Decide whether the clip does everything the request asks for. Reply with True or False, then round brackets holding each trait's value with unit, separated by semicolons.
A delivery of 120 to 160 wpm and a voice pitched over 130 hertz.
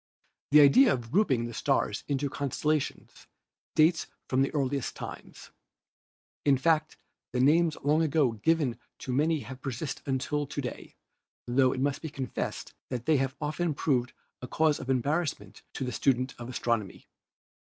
True (155 wpm; 140 Hz)